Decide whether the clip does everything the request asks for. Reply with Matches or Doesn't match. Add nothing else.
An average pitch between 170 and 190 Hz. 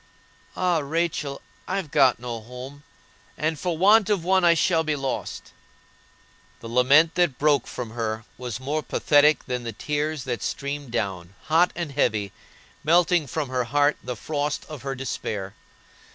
Doesn't match